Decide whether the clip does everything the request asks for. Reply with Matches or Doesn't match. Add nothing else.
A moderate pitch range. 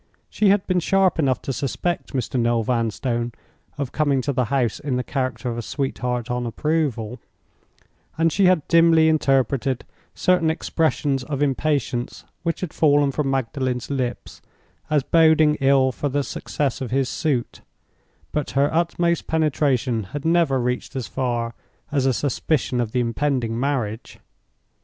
Matches